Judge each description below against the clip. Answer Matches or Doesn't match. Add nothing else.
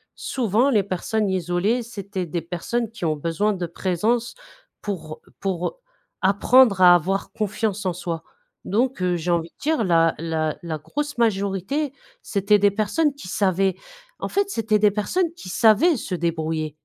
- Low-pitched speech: Doesn't match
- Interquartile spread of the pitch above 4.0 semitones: Matches